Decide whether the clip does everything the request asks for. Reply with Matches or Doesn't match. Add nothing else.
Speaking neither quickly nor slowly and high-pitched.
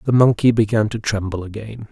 Doesn't match